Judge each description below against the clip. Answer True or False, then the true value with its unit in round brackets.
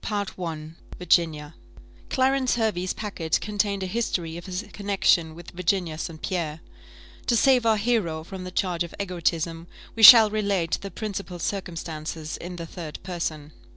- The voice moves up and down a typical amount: True (3.7 semitones)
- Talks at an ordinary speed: True (155 wpm)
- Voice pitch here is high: False (180 Hz)